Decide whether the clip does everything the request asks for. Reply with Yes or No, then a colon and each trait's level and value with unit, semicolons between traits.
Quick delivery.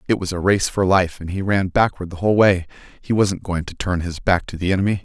Yes: fast, 275 wpm